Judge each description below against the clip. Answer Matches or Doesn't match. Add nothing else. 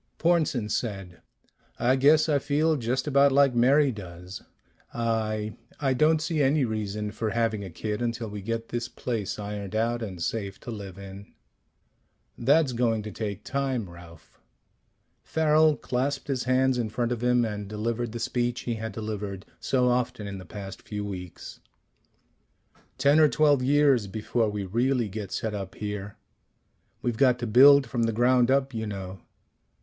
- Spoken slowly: Doesn't match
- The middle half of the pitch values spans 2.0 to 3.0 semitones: Doesn't match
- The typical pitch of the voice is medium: Doesn't match